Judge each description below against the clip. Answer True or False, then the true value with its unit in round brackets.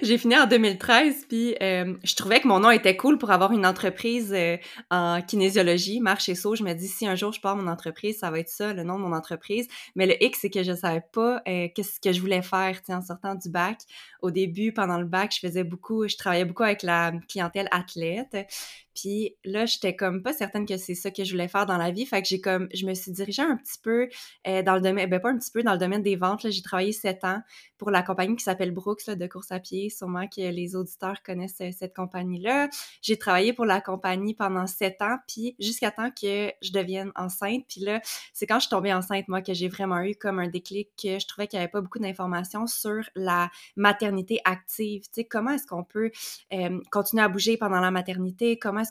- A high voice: True (195 Hz)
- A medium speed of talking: False (240 wpm)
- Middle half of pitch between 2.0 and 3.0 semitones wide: True (2.7 semitones)